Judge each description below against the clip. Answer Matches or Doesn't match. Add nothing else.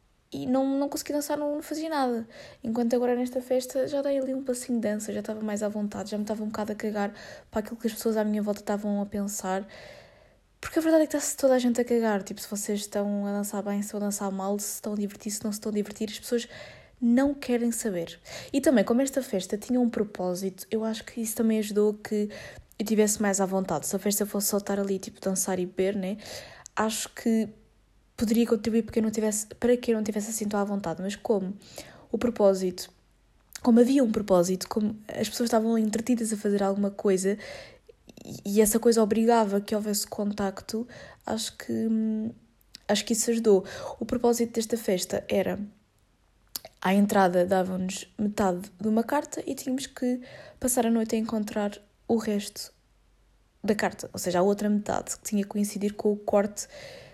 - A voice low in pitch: Doesn't match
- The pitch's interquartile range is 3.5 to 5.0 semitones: Doesn't match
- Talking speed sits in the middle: Doesn't match